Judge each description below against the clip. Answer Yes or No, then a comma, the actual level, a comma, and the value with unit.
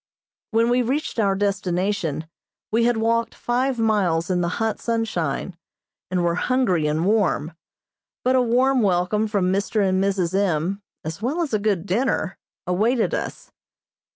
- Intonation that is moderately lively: Yes, average, 4.4 semitones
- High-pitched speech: Yes, high, 205 Hz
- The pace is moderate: Yes, average, 155 wpm